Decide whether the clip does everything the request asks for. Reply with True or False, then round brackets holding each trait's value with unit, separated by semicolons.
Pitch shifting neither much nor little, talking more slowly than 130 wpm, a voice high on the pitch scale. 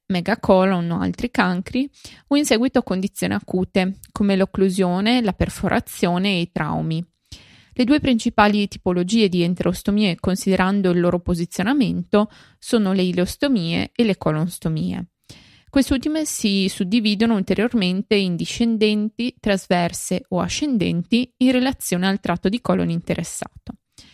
True (4.4 semitones; 120 wpm; 200 Hz)